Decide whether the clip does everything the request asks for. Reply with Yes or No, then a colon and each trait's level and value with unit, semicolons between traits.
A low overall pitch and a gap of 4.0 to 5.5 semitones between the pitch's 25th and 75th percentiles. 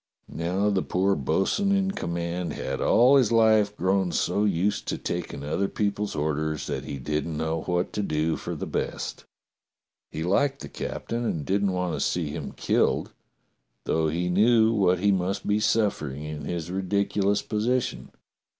Yes: very low, 95 Hz; average, 4.4 semitones